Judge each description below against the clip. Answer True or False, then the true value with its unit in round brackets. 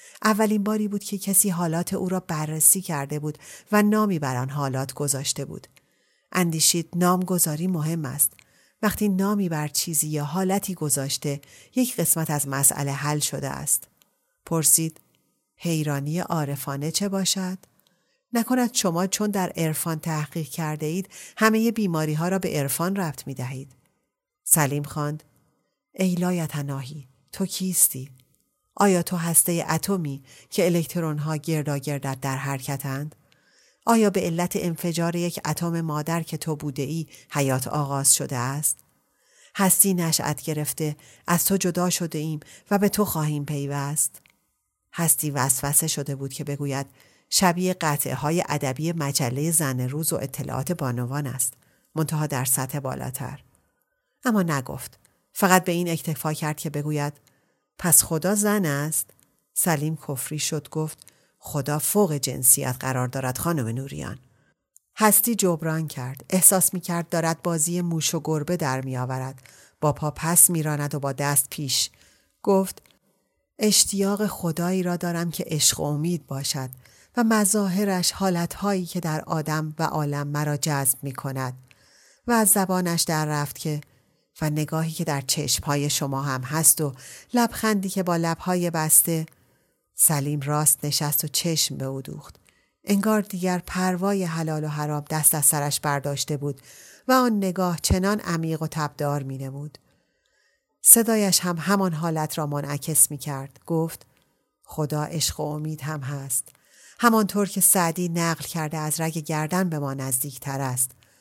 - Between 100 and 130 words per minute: False (145 wpm)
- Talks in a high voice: False (155 Hz)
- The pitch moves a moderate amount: True (4.0 semitones)